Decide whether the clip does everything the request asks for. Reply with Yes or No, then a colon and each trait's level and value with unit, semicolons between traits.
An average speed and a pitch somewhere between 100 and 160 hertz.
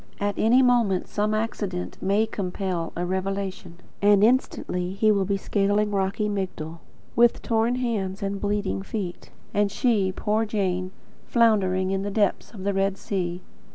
No: average, 155 wpm; high, 200 Hz